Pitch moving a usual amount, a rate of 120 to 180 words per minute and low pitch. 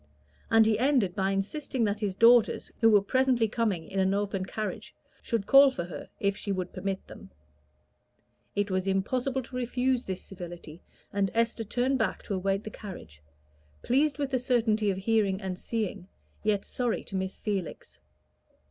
No: average, 3.9 semitones; average, 170 wpm; high, 210 Hz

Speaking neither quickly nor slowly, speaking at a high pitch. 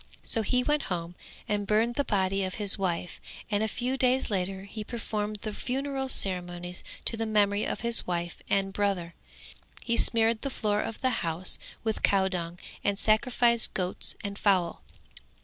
Yes: average, 165 wpm; high, 205 Hz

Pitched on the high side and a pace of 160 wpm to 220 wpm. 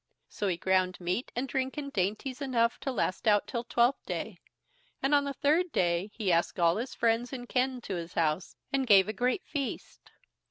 Yes: high, 235 Hz; average, 200 wpm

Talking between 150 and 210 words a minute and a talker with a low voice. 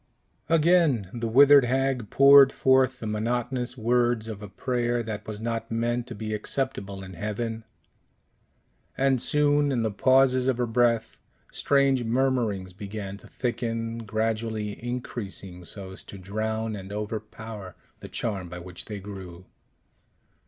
No: average, 140 wpm; low, 115 Hz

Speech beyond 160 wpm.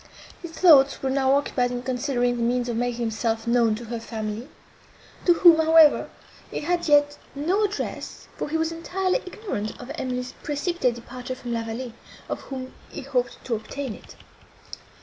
Yes: average, 170 wpm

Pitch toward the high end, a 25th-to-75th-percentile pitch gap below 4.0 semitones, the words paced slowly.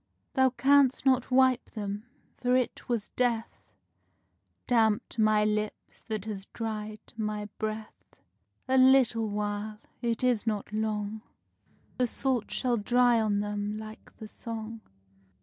Yes: high, 220 Hz; average, 2.7 semitones; slow, 130 wpm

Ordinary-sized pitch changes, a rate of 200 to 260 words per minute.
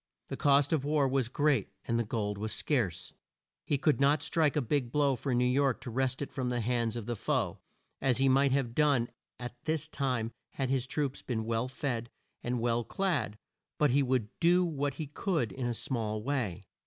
Yes: average, 3.4 semitones; fast, 205 wpm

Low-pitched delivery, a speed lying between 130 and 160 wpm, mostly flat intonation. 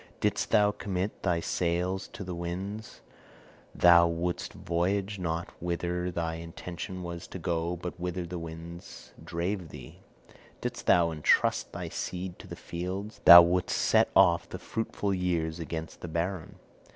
Yes: very low, 85 Hz; average, 150 wpm; narrow, 1.6 semitones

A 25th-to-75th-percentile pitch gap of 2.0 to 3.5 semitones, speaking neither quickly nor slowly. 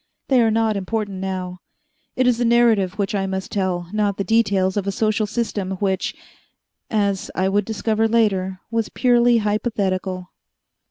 Yes: average, 2.8 semitones; average, 160 wpm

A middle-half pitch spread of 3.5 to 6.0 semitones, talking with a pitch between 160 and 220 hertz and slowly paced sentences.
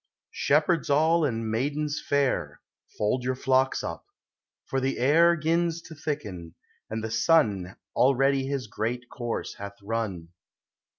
No: average, 5.1 semitones; low, 130 Hz; slow, 130 wpm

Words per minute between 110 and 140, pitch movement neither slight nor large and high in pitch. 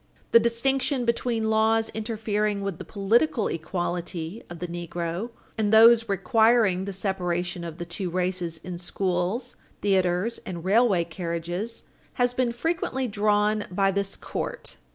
Yes: slow, 135 wpm; average, 4.4 semitones; high, 200 Hz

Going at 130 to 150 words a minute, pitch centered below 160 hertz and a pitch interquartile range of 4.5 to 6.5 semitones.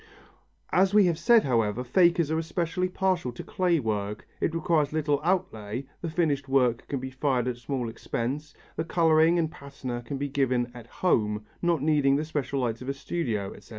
No: average, 185 wpm; medium, 140 Hz; average, 5.3 semitones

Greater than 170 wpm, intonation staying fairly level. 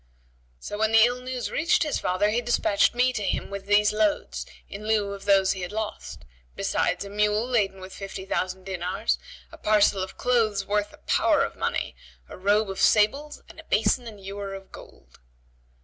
Yes: average, 195 wpm; narrow, 2.1 semitones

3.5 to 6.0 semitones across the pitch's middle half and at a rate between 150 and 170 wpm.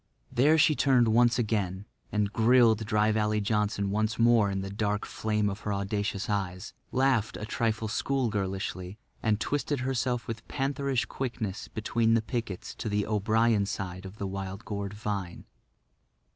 No: narrow, 2.6 semitones; average, 155 wpm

